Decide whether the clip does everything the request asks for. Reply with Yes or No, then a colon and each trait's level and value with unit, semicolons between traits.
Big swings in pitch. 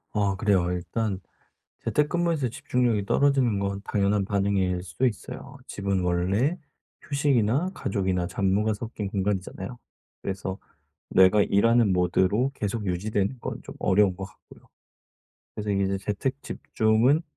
No: average, 3.7 semitones